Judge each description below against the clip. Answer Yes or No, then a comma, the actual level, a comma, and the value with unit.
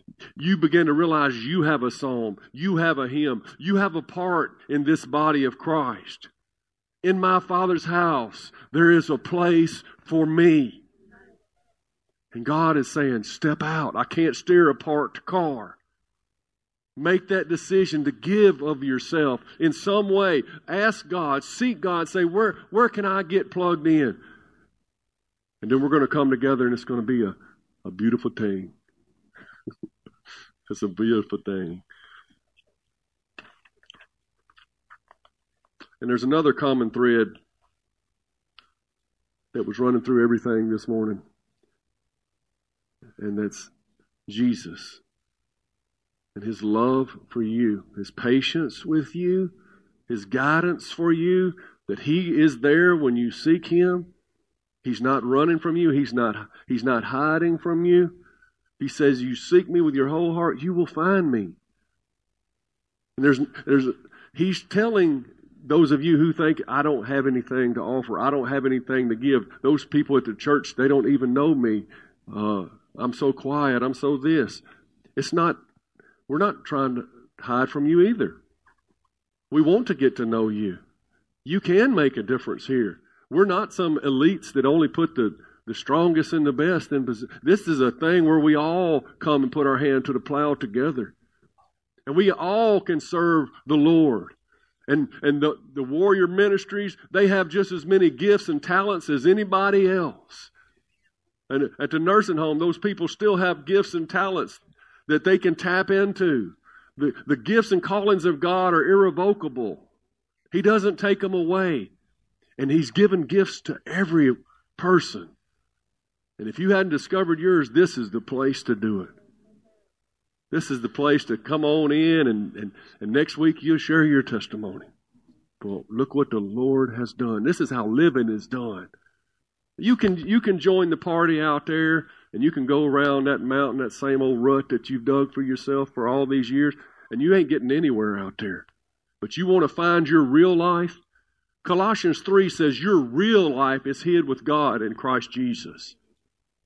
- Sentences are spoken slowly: No, average, 165 wpm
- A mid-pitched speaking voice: Yes, medium, 150 Hz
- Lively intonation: Yes, wide, 5.8 semitones